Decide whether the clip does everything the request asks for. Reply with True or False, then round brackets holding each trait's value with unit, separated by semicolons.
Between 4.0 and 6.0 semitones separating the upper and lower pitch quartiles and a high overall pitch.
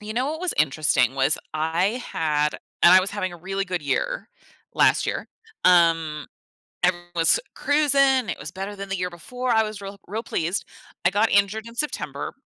True (5.1 semitones; 195 Hz)